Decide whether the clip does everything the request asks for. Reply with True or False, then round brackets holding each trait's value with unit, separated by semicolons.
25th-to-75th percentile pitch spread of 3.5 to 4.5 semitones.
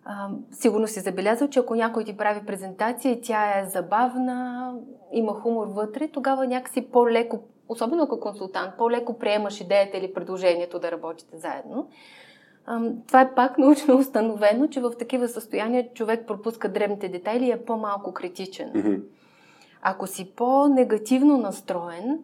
True (3.9 semitones)